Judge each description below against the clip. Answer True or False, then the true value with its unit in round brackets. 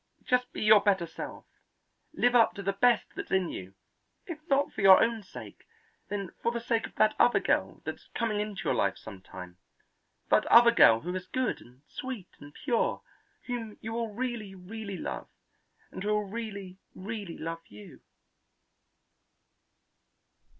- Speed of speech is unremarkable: True (165 wpm)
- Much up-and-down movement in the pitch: False (4.4 semitones)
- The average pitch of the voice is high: True (210 Hz)